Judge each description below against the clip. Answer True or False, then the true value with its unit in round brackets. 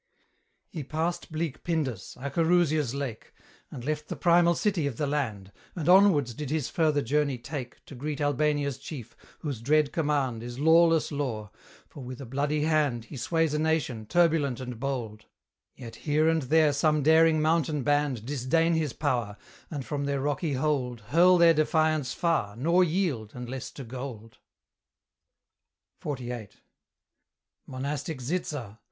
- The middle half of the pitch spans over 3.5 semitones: True (3.9 semitones)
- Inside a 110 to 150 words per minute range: True (145 wpm)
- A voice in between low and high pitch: True (145 Hz)